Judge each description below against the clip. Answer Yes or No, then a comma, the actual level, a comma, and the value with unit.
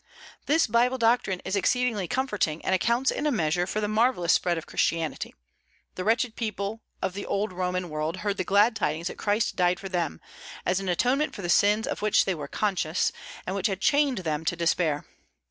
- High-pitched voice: Yes, high, 195 Hz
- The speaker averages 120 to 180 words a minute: No, average, 200 wpm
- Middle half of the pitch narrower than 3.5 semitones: No, average, 4.3 semitones